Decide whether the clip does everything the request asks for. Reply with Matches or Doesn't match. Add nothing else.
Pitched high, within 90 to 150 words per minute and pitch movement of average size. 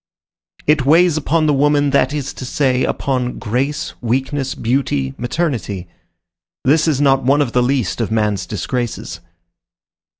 Doesn't match